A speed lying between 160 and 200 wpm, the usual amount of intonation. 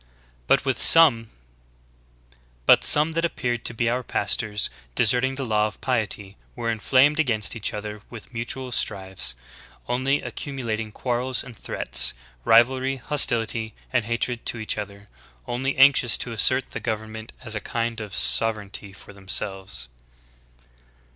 No: slow, 135 wpm; average, 3.3 semitones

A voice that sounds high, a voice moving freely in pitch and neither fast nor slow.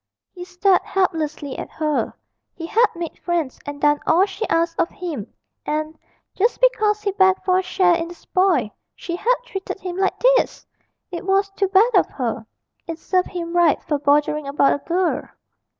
No: very high, 350 Hz; average, 3.9 semitones; average, 180 wpm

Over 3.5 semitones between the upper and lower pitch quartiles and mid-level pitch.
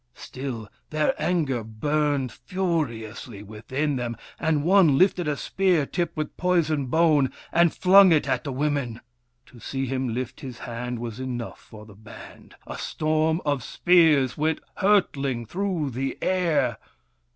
Yes: average, 4.9 semitones; medium, 145 Hz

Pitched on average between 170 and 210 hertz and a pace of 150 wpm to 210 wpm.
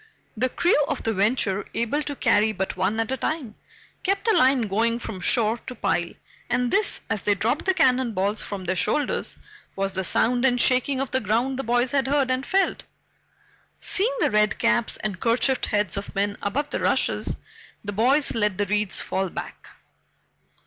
No: high, 230 Hz; average, 190 wpm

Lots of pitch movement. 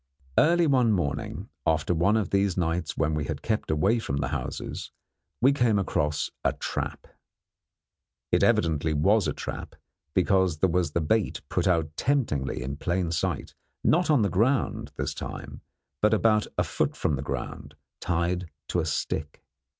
Yes: wide, 5.9 semitones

